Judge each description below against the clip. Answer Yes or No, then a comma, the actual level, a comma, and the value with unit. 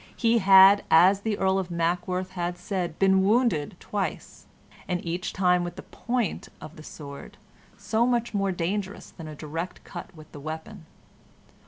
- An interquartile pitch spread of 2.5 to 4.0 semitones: Yes, average, 3.1 semitones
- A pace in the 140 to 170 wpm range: Yes, average, 165 wpm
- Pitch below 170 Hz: No, medium, 185 Hz